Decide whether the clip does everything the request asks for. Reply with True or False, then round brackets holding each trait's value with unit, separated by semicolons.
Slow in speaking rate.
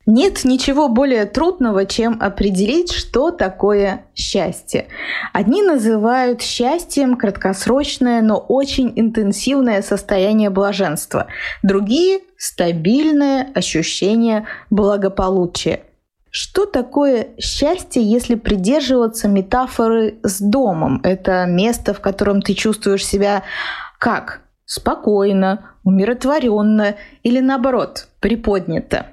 True (90 wpm)